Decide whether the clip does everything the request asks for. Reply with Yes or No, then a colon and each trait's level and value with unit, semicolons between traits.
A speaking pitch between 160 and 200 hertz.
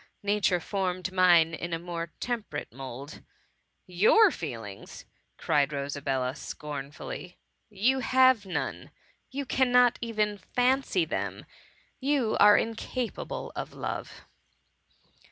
Yes: medium, 185 Hz